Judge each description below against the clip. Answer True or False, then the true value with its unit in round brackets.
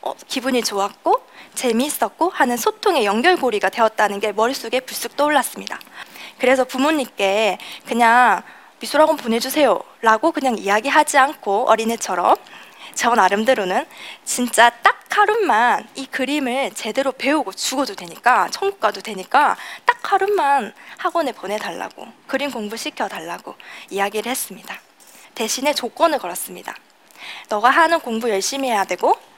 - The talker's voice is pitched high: True (250 Hz)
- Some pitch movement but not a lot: True (4.9 semitones)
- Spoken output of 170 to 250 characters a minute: False (330 characters per minute)